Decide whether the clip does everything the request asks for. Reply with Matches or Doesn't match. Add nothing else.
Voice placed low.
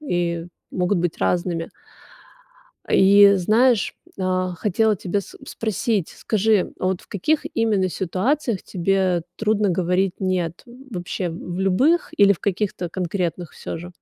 Doesn't match